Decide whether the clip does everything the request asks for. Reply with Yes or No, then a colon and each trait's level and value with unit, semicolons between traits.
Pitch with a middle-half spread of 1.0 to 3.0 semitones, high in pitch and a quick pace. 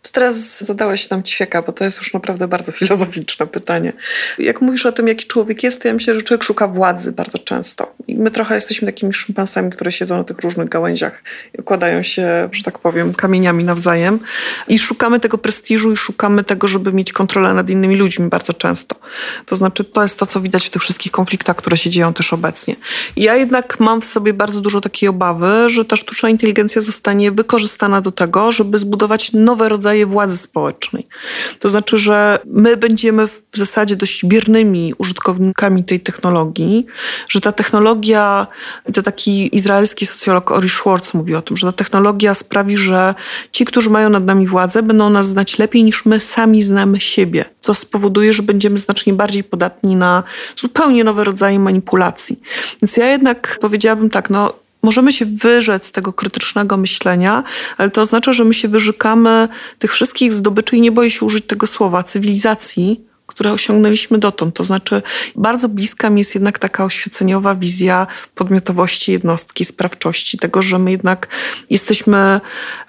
Yes: narrow, 2.5 semitones; high, 205 Hz; fast, 175 wpm